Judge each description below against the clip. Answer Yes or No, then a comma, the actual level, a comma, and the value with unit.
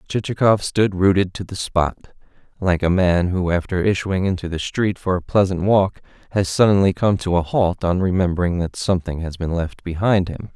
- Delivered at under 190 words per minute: No, average, 195 wpm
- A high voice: No, very low, 90 Hz